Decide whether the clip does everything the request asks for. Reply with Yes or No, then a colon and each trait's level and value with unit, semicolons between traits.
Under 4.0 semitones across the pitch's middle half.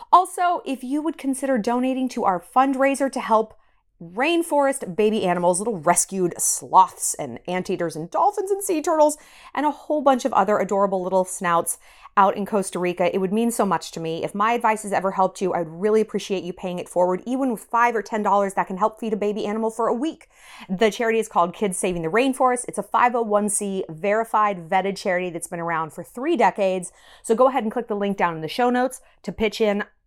No: average, 5.0 semitones